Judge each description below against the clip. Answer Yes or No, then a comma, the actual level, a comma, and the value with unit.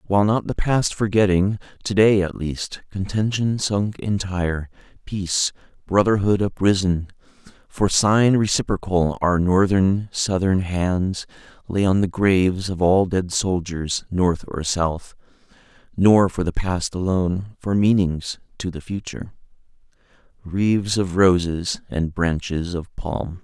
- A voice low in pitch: Yes, very low, 95 Hz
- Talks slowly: Yes, slow, 125 wpm